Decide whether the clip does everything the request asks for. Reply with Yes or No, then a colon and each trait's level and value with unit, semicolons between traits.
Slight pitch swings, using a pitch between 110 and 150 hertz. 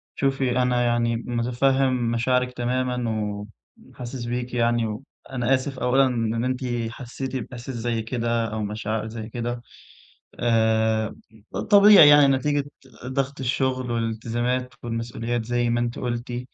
Yes: narrow, 1.8 semitones; low, 120 Hz